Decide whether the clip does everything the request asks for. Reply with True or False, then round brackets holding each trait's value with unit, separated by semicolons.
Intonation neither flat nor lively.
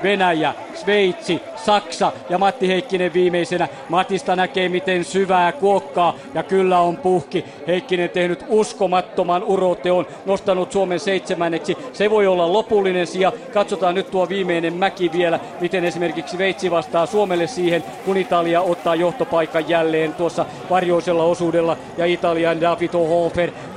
False (1.9 semitones)